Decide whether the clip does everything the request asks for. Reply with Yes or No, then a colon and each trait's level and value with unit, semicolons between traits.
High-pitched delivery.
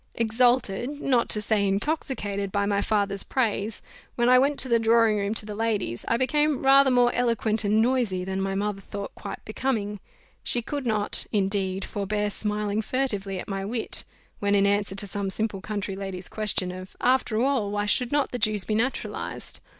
Yes: high, 210 Hz